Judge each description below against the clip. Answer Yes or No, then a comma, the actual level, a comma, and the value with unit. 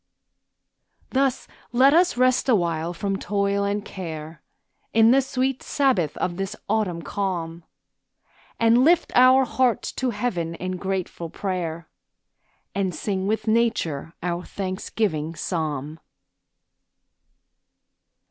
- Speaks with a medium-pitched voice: No, high, 195 Hz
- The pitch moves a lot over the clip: Yes, wide, 6.1 semitones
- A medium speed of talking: No, slow, 110 wpm